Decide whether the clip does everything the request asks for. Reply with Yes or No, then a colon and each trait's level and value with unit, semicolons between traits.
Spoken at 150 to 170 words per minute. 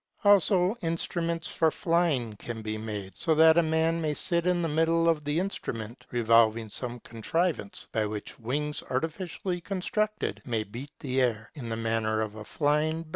No: average, 180 wpm